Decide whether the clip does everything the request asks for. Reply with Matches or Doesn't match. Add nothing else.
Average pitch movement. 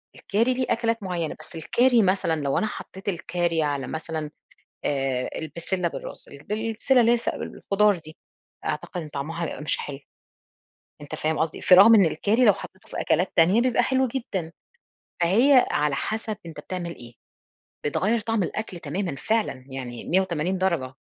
Doesn't match